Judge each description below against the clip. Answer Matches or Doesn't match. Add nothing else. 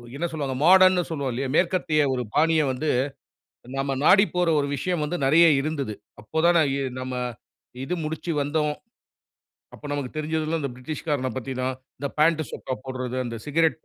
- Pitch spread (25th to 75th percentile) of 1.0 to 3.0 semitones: Doesn't match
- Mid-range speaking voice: Matches